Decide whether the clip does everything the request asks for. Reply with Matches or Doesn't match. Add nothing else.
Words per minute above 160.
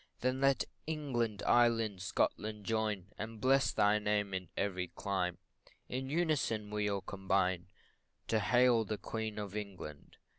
Doesn't match